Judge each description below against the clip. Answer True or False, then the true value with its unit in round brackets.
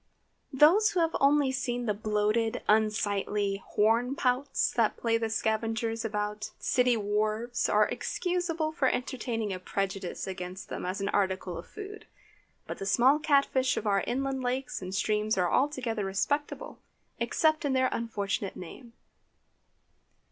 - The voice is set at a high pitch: True (225 Hz)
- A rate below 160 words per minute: True (145 wpm)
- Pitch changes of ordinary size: True (4.4 semitones)